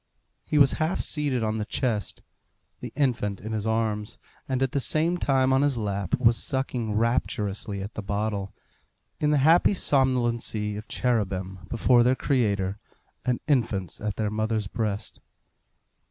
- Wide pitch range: No, average, 4.1 semitones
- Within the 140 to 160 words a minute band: Yes, average, 155 wpm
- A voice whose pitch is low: Yes, low, 115 Hz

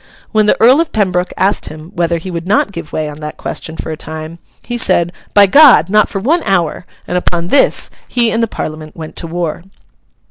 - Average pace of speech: No, fast, 215 wpm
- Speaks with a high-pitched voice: No, medium, 175 Hz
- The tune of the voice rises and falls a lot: No, average, 4.9 semitones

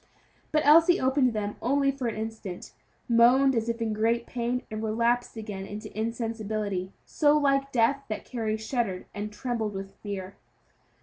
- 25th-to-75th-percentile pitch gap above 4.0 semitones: No, average, 3.3 semitones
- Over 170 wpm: No, average, 160 wpm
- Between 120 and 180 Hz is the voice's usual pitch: No, high, 230 Hz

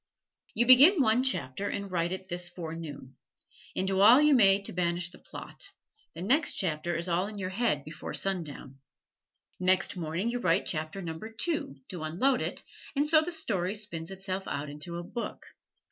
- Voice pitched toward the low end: No, medium, 185 Hz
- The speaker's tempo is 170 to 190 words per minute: Yes, average, 180 wpm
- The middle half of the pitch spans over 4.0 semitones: Yes, average, 5.2 semitones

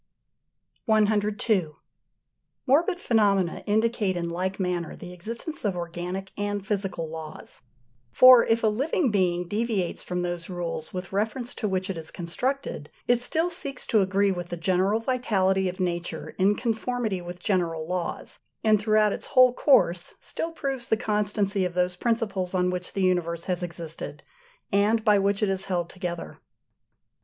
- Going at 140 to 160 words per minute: Yes, average, 155 wpm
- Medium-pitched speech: No, high, 195 Hz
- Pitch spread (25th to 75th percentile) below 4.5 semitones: Yes, average, 3.8 semitones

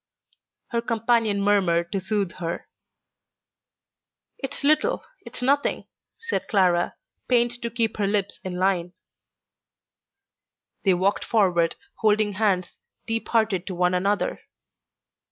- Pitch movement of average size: Yes, average, 3.9 semitones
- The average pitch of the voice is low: No, high, 205 Hz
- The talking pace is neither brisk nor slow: No, slow, 115 wpm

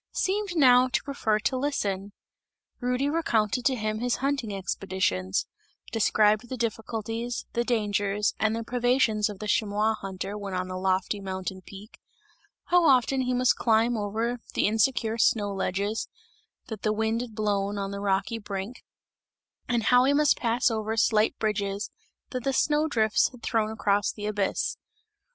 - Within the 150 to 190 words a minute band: Yes, average, 160 wpm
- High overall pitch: Yes, high, 220 Hz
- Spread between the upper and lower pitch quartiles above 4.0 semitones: No, average, 3.4 semitones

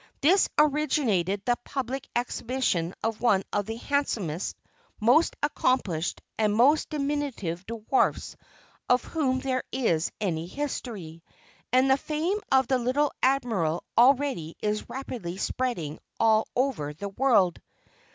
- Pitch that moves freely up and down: Yes, wide, 5.9 semitones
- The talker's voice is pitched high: Yes, high, 245 Hz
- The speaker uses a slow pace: Yes, slow, 120 wpm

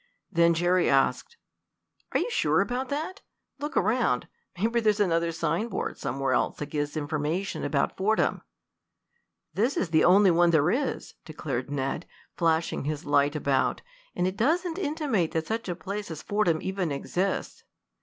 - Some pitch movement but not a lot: No, wide, 6.3 semitones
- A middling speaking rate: Yes, average, 155 wpm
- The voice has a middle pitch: Yes, medium, 175 Hz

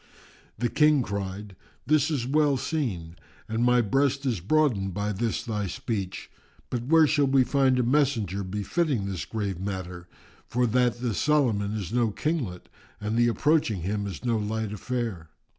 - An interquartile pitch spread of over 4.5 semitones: Yes, average, 5.2 semitones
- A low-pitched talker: Yes, low, 115 Hz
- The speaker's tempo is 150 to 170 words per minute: Yes, average, 160 wpm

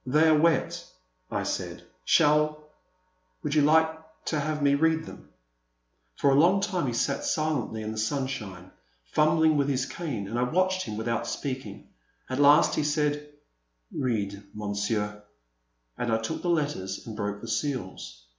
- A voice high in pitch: No, medium, 140 Hz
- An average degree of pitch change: No, wide, 5.9 semitones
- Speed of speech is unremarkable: Yes, average, 165 wpm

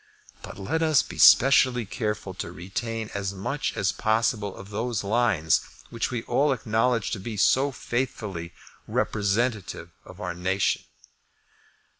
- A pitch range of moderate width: Yes, average, 4.0 semitones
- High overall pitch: No, low, 110 Hz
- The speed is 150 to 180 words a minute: No, slow, 135 wpm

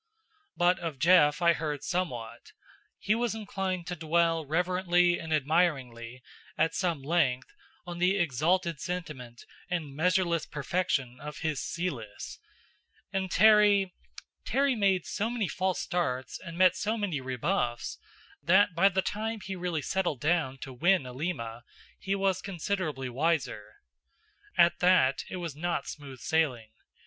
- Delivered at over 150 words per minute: No, slow, 135 wpm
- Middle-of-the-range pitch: Yes, medium, 170 Hz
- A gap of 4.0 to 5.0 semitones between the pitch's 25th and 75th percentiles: Yes, average, 4.7 semitones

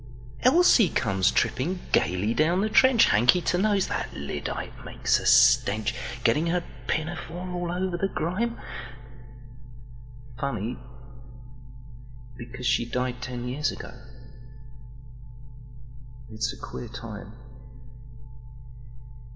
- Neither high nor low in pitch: No, low, 125 Hz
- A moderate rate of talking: No, slow, 85 wpm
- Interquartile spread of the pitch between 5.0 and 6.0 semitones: Yes, wide, 5.4 semitones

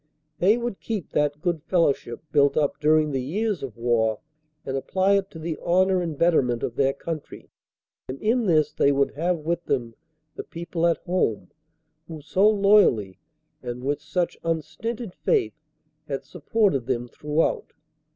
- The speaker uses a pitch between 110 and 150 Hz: No, medium, 160 Hz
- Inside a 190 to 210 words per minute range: No, average, 160 wpm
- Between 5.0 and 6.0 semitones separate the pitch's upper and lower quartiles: Yes, wide, 5.4 semitones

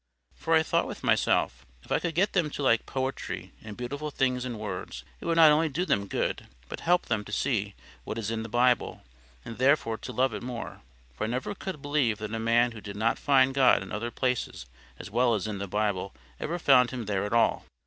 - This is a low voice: Yes, low, 120 Hz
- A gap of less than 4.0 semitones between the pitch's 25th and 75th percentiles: No, average, 4.5 semitones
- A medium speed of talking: No, fast, 230 wpm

